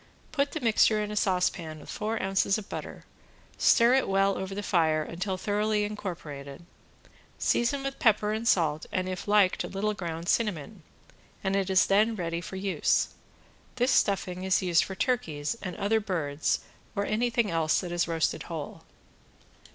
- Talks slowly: No, average, 165 wpm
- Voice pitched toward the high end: Yes, high, 195 Hz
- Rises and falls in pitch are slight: No, average, 3.7 semitones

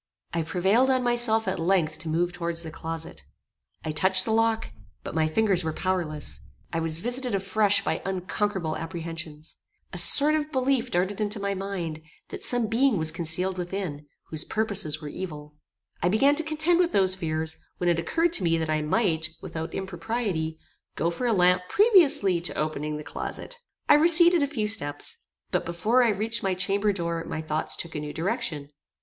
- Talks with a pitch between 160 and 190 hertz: Yes, medium, 185 Hz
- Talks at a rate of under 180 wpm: No, average, 185 wpm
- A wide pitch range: Yes, wide, 5.7 semitones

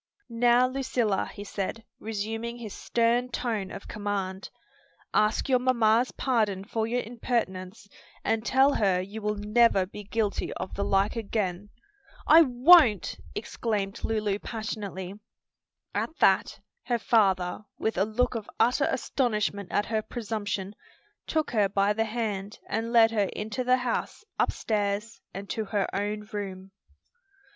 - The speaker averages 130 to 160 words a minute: Yes, average, 140 wpm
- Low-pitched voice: No, high, 215 Hz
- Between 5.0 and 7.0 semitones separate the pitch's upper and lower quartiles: No, average, 2.7 semitones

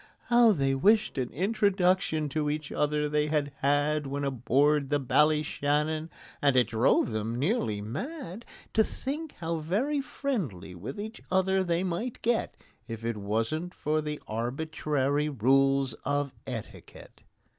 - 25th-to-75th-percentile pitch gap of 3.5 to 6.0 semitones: Yes, average, 5.3 semitones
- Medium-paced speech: Yes, average, 145 wpm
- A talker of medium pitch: Yes, medium, 150 Hz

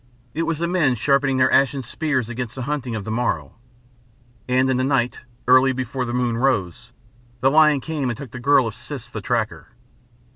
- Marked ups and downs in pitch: No, narrow, 2.4 semitones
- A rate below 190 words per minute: No, average, 195 wpm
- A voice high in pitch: No, low, 130 Hz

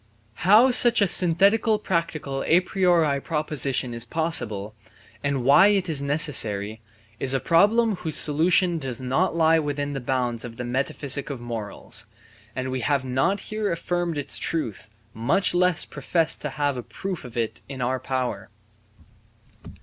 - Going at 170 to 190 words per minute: No, average, 155 wpm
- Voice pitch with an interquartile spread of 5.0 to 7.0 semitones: Yes, wide, 5.5 semitones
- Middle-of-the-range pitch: Yes, medium, 145 Hz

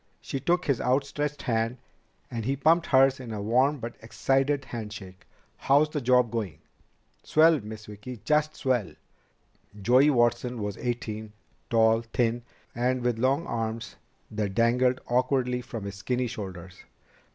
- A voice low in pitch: Yes, low, 120 Hz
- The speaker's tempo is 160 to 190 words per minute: No, average, 140 wpm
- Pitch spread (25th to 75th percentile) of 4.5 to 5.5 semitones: No, average, 3.2 semitones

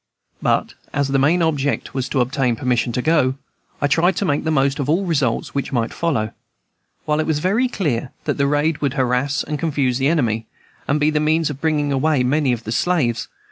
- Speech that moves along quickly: Yes, fast, 215 wpm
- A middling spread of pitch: Yes, average, 3.4 semitones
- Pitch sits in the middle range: Yes, medium, 145 Hz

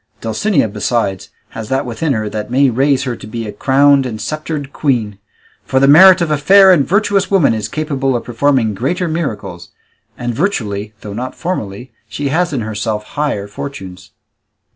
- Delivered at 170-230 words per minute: Yes, average, 175 wpm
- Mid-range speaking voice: No, low, 130 Hz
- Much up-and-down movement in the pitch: Yes, wide, 5.8 semitones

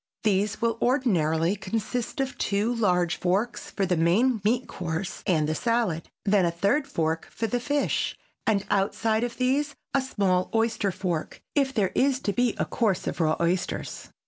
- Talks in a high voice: Yes, high, 205 Hz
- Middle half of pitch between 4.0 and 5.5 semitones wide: Yes, average, 5.2 semitones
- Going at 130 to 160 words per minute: No, average, 170 wpm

